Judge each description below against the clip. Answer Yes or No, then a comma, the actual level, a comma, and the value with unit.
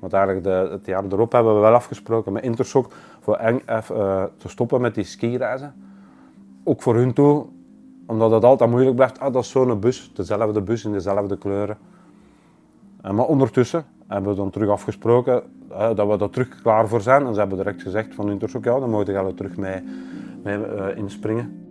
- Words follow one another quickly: No, average, 180 wpm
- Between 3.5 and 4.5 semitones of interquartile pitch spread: Yes, average, 3.9 semitones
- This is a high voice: No, low, 105 Hz